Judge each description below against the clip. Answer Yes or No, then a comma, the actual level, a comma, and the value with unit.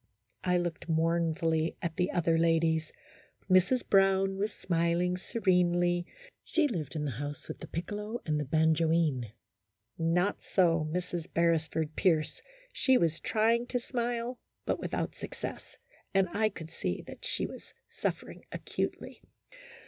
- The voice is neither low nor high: Yes, medium, 170 Hz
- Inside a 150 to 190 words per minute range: No, average, 140 wpm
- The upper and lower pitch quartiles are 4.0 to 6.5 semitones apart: No, average, 3.2 semitones